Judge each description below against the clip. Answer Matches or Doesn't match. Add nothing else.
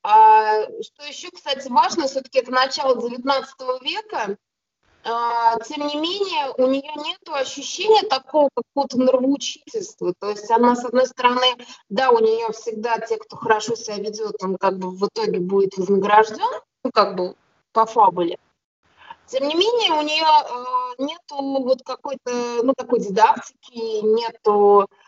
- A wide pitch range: Doesn't match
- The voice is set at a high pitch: Matches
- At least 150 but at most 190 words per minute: Doesn't match